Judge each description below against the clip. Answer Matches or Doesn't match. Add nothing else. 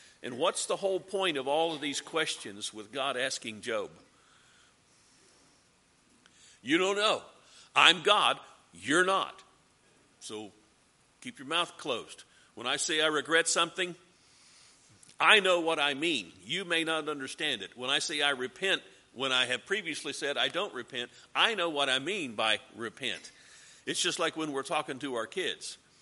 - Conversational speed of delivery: Matches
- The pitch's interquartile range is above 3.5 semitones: Matches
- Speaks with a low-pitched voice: Doesn't match